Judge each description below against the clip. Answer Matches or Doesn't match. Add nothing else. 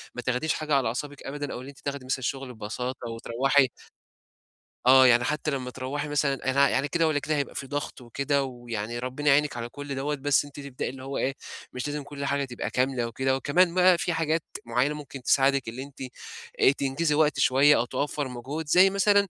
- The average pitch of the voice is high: Doesn't match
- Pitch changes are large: Doesn't match